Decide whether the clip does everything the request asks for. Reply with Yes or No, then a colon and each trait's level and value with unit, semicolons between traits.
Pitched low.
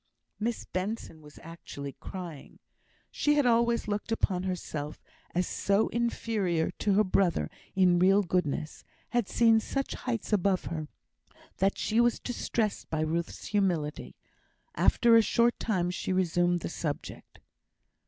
No: high, 190 Hz